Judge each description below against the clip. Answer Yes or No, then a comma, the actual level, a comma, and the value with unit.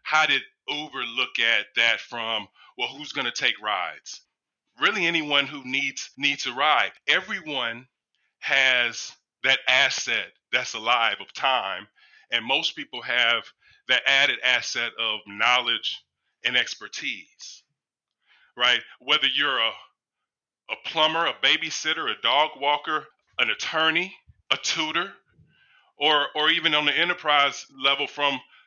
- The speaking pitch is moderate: Yes, medium, 145 Hz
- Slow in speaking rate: Yes, slow, 130 wpm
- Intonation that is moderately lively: Yes, average, 3.1 semitones